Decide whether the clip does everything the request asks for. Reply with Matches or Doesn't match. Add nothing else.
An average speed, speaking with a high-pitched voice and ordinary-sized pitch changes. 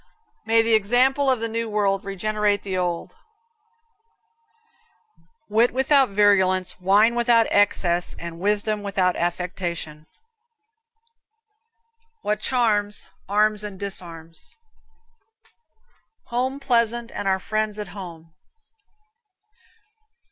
Doesn't match